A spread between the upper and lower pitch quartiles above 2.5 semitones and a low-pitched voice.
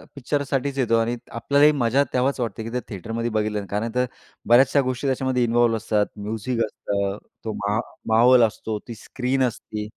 Yes: average, 2.9 semitones; low, 120 Hz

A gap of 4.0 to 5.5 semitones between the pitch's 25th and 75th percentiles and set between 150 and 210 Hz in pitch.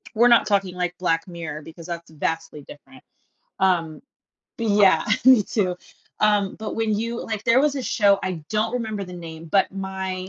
Yes: average, 4.3 semitones; high, 190 Hz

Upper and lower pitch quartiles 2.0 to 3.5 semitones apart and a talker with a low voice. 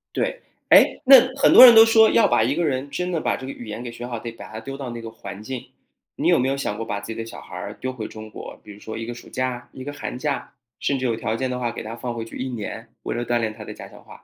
Yes: average, 3.2 semitones; low, 120 Hz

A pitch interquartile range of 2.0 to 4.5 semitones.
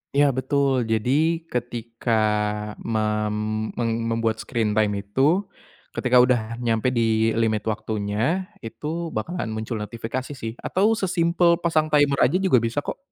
No: average, 5.0 semitones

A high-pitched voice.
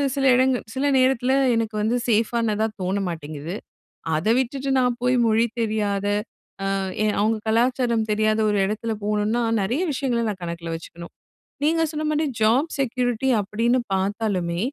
Yes: high, 225 Hz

